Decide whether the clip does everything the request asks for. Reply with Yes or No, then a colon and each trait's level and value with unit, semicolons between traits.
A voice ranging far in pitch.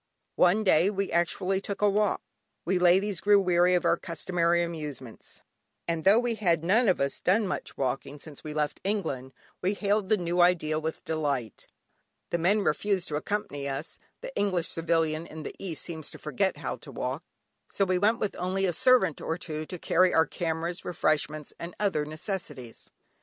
No: average, 4.0 semitones